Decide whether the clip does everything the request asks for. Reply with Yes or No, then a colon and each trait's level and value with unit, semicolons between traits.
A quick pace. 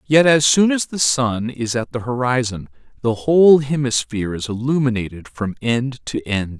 No: average, 175 wpm